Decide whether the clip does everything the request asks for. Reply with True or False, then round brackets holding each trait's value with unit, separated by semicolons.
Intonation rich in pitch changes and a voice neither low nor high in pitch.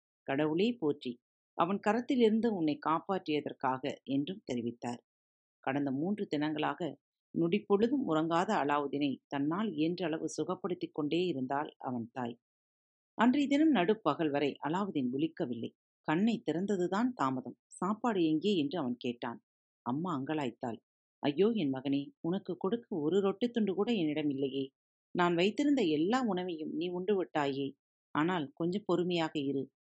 True (6.3 semitones; 155 Hz)